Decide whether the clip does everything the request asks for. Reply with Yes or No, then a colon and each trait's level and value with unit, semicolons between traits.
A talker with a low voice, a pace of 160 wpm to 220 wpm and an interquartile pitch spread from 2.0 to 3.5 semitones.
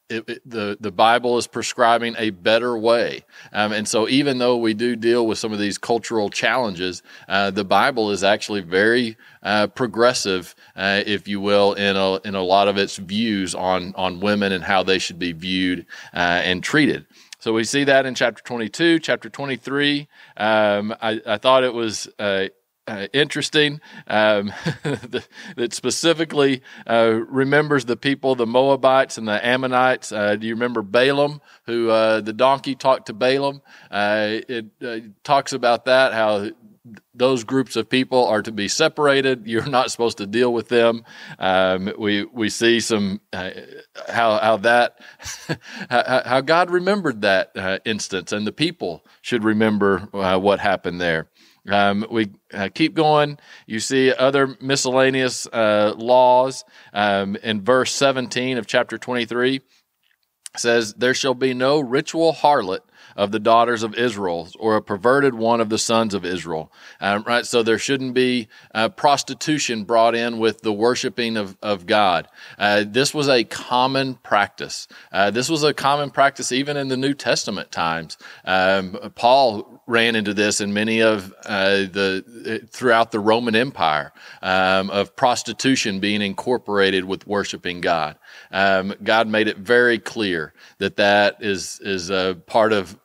No: low, 115 Hz; average, 165 wpm; average, 4.1 semitones